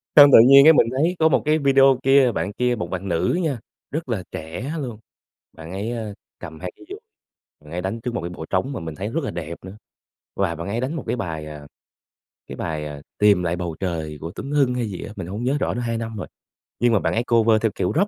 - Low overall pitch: Yes, low, 110 Hz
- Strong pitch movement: Yes, wide, 7.3 semitones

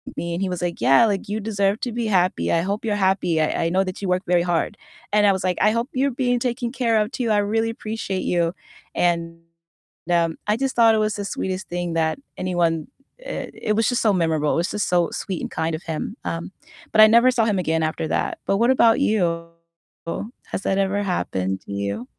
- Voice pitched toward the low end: No, high, 190 Hz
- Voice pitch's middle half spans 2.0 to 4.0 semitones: No, average, 4.6 semitones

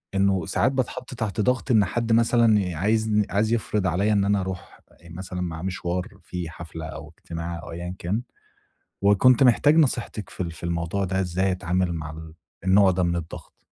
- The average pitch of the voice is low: Yes, very low, 95 Hz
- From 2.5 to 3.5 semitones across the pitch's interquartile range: No, average, 3.9 semitones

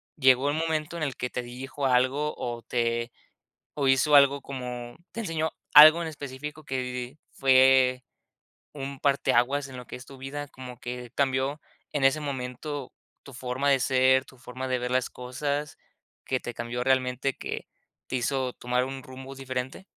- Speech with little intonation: Yes, narrow, 2.1 semitones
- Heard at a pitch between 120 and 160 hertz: Yes, low, 130 Hz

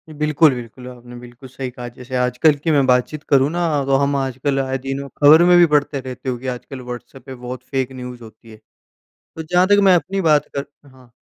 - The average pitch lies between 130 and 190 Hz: Yes, low, 135 Hz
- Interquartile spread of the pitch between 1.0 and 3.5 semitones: Yes, average, 2.8 semitones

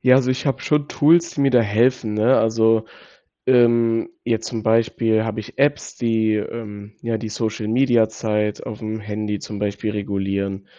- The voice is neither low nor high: No, low, 110 Hz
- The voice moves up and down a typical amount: No, narrow, 2.1 semitones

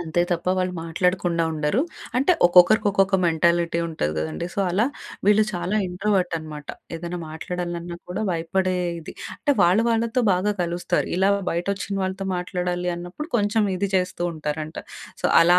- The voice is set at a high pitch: No, medium, 180 Hz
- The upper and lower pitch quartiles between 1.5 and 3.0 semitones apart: Yes, narrow, 2.4 semitones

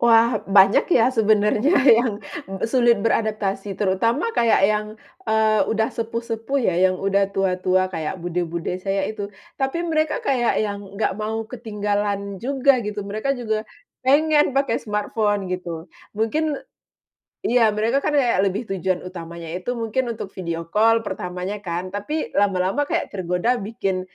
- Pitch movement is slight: No, average, 3.5 semitones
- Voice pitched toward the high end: Yes, high, 210 Hz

